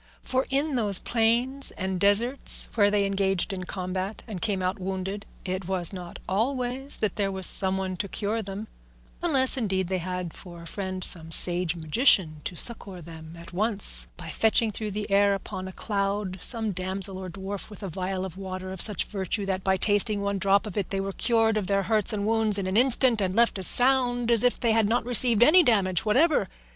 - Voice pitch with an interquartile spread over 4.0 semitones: No, average, 3.1 semitones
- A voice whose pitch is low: No, high, 200 Hz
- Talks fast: Yes, fast, 210 wpm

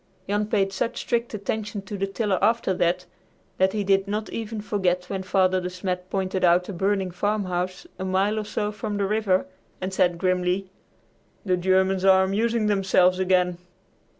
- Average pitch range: No, narrow, 2.0 semitones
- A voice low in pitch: No, high, 190 Hz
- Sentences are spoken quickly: No, average, 175 wpm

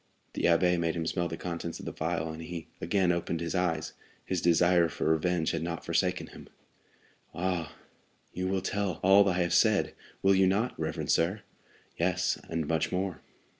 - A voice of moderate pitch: No, very low, 85 Hz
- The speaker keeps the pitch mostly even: Yes, narrow, 2.0 semitones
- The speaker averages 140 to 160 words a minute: No, average, 180 wpm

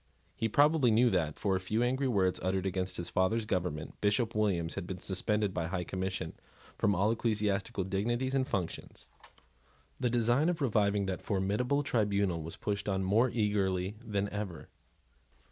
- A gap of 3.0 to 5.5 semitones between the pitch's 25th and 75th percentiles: Yes, average, 3.5 semitones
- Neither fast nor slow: Yes, average, 165 wpm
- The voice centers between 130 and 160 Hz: No, low, 100 Hz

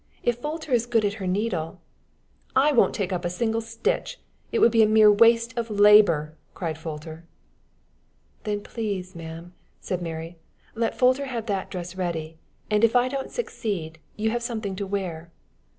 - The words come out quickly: No, average, 170 wpm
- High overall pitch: Yes, high, 205 Hz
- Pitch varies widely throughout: No, average, 5.0 semitones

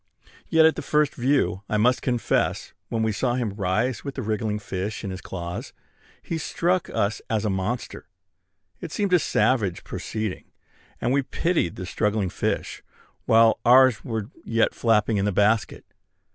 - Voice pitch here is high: No, low, 110 Hz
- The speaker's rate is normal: Yes, average, 160 wpm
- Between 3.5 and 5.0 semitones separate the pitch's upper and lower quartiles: Yes, average, 3.9 semitones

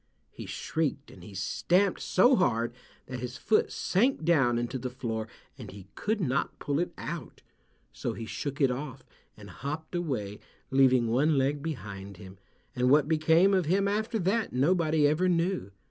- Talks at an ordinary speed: Yes, average, 170 wpm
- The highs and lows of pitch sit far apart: Yes, wide, 6.2 semitones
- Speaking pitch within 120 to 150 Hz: Yes, medium, 140 Hz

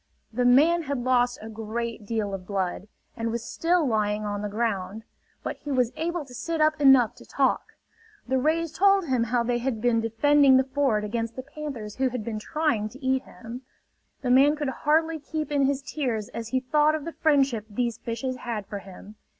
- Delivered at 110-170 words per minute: No, fast, 205 wpm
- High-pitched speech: Yes, very high, 250 Hz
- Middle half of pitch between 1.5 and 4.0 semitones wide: No, average, 4.6 semitones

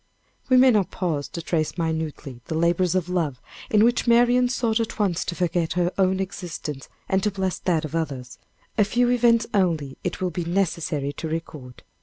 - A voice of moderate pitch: Yes, medium, 180 Hz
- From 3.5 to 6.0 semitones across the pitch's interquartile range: Yes, average, 4.6 semitones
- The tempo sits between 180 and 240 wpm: Yes, average, 190 wpm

